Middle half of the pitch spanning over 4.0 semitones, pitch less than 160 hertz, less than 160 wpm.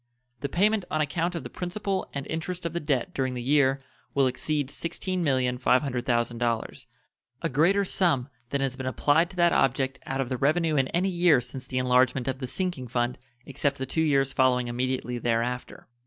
No: average, 4.6 semitones; low, 135 Hz; average, 185 wpm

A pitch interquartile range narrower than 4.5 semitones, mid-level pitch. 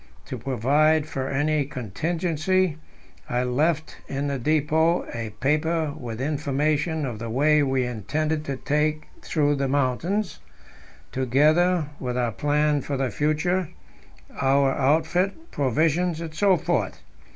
Yes: average, 3.0 semitones; medium, 150 Hz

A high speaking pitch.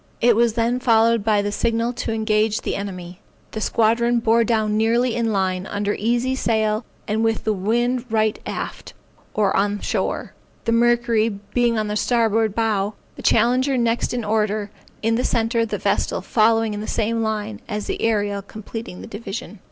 Yes: high, 220 Hz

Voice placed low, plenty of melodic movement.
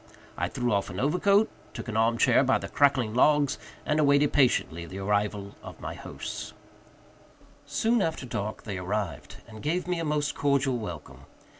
Yes: low, 130 Hz; wide, 5.9 semitones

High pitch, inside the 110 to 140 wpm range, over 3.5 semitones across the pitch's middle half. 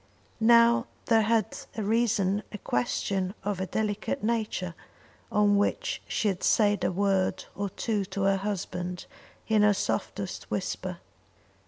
No: high, 205 Hz; slow, 135 wpm; narrow, 2.5 semitones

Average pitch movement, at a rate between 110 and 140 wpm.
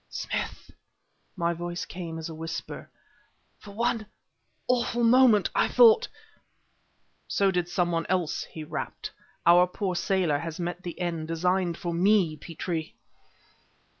Yes: average, 3.0 semitones; slow, 135 wpm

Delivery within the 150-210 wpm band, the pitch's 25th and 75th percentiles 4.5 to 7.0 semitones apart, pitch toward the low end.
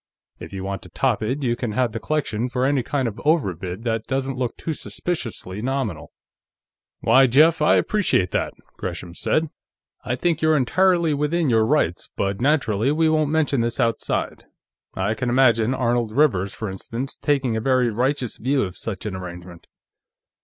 Yes: average, 175 wpm; average, 5.1 semitones; low, 125 Hz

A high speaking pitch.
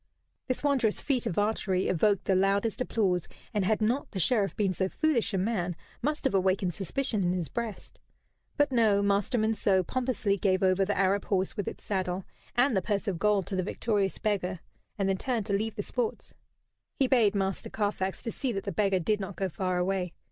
Yes: high, 200 Hz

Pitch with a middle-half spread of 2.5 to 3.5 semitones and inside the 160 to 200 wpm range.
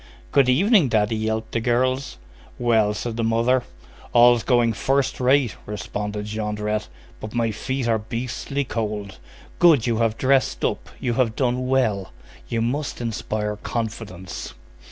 No: average, 3.1 semitones; average, 140 wpm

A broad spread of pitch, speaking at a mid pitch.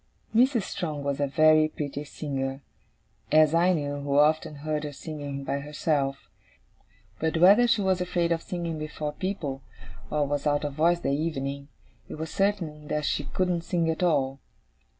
No: average, 3.0 semitones; medium, 155 Hz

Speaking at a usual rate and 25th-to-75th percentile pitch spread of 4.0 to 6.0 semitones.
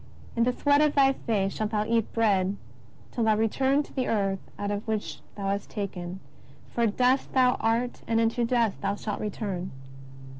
No: average, 185 wpm; average, 3.3 semitones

